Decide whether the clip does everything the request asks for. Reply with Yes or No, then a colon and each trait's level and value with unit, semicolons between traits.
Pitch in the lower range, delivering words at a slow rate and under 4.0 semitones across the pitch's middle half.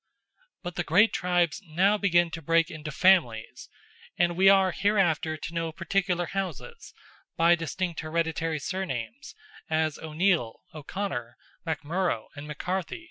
No: medium, 170 Hz; slow, 130 wpm; average, 3.1 semitones